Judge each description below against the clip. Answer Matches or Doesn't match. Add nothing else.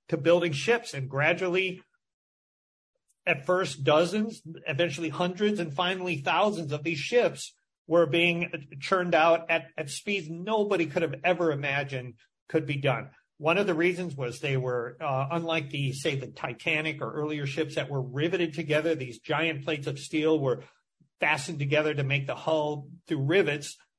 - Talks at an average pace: Matches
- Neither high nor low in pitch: Matches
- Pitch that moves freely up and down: Doesn't match